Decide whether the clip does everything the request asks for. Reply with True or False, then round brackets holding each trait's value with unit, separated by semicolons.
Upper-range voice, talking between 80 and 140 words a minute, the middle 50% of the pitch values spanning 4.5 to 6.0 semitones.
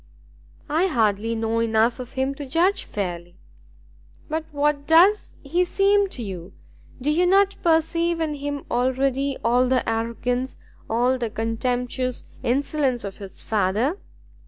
True (260 Hz; 135 wpm; 5.4 semitones)